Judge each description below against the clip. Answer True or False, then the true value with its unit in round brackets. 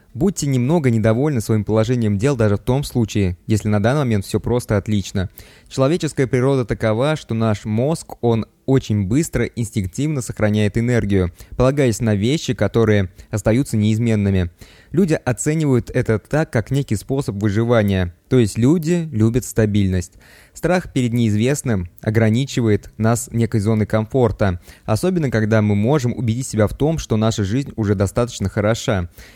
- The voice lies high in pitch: False (115 Hz)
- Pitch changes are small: False (3.5 semitones)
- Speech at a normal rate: True (145 wpm)